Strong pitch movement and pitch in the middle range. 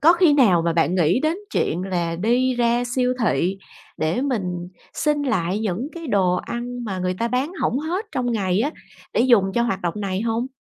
No: wide, 5.8 semitones; high, 230 Hz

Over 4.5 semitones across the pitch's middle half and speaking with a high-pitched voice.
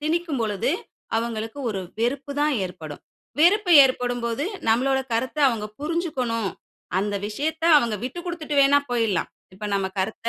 Yes: average, 5.2 semitones; high, 245 Hz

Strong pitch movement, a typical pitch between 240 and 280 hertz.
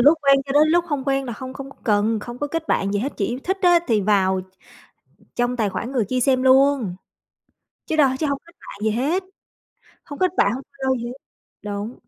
No: average, 4.6 semitones; very high, 260 Hz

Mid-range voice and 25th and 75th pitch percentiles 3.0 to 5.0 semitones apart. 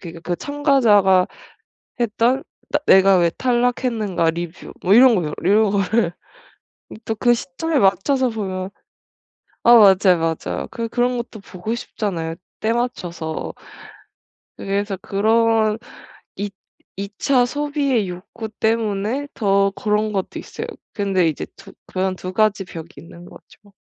No: high, 210 Hz; average, 4.1 semitones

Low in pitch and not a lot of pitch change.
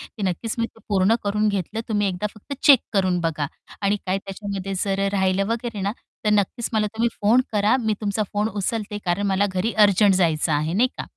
No: high, 200 Hz; narrow, 2.1 semitones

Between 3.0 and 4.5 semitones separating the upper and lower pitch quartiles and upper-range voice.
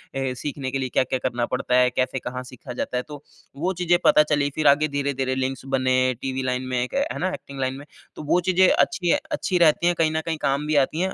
No: average, 3.5 semitones; medium, 140 Hz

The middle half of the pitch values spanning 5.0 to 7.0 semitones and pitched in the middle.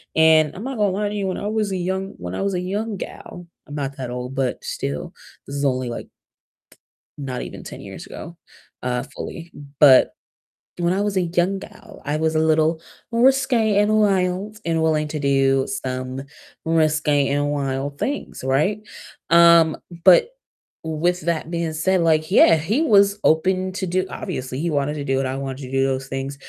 Yes: wide, 5.4 semitones; medium, 160 Hz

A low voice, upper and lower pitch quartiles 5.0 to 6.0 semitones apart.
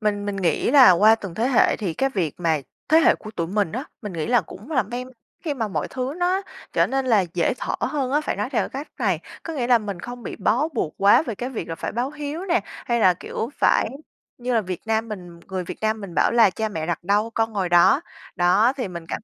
No: high, 220 Hz; wide, 5.5 semitones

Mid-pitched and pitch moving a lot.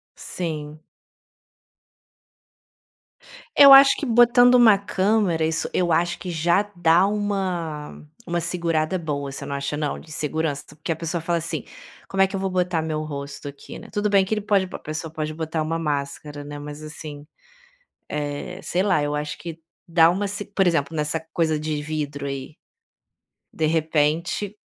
No: medium, 160 Hz; average, 3.8 semitones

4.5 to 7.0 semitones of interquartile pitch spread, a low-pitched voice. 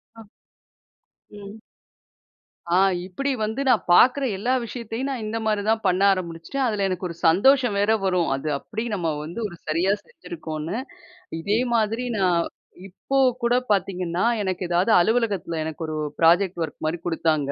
No: average, 4.8 semitones; high, 195 Hz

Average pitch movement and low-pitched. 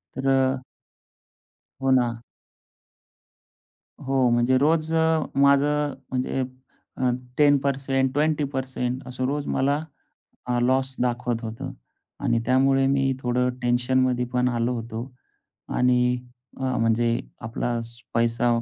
No: narrow, 1.9 semitones; low, 130 Hz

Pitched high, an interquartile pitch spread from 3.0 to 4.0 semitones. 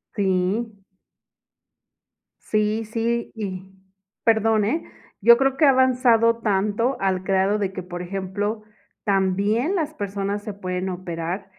Yes: high, 205 Hz; average, 3.3 semitones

